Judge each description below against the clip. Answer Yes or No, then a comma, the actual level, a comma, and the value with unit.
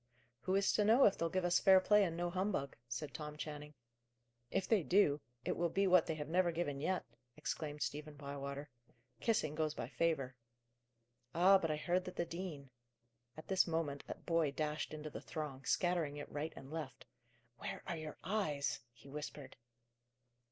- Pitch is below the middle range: No, medium, 155 Hz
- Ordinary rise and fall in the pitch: Yes, average, 3.8 semitones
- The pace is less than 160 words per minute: No, average, 185 wpm